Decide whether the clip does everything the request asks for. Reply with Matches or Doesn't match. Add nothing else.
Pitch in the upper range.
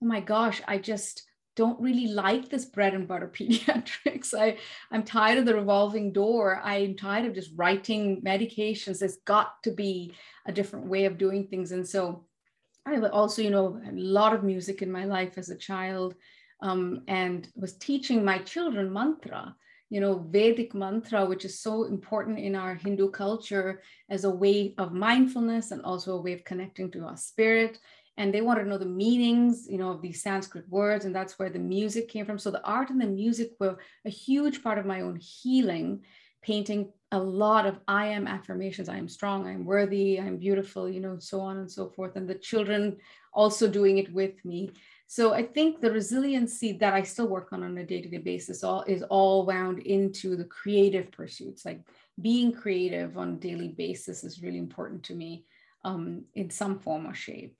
Matches